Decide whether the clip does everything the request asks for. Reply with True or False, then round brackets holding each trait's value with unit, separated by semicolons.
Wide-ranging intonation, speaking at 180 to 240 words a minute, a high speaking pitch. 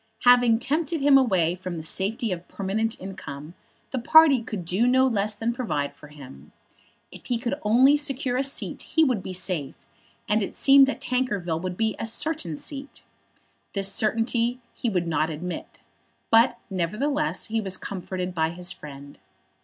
False (5.9 semitones; 170 wpm; 215 Hz)